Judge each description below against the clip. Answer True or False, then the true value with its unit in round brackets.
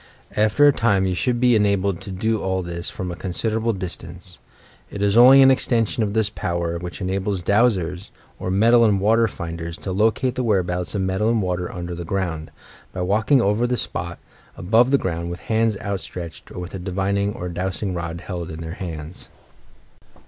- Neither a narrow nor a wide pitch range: True (3.9 semitones)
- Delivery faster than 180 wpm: True (190 wpm)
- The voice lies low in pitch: True (95 Hz)